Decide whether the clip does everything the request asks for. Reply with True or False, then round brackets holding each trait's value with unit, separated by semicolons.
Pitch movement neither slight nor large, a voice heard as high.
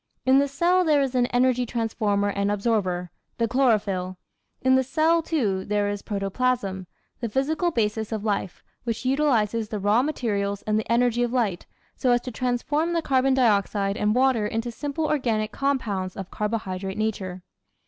True (4.3 semitones; 230 Hz)